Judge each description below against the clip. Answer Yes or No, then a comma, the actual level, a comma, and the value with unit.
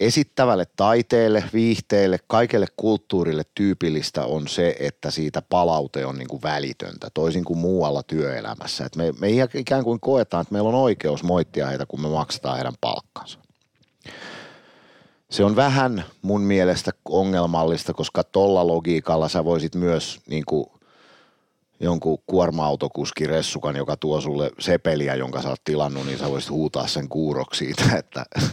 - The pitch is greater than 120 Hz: No, very low, 80 Hz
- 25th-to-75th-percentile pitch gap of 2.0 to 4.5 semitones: No, average, 4.9 semitones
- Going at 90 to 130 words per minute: No, average, 145 wpm